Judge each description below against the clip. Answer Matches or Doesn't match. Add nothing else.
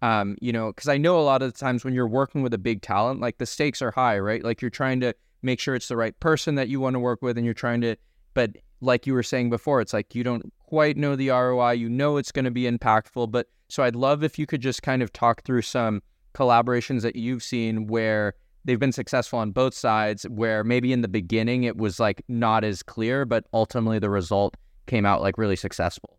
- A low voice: Matches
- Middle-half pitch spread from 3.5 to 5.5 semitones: Doesn't match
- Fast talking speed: Matches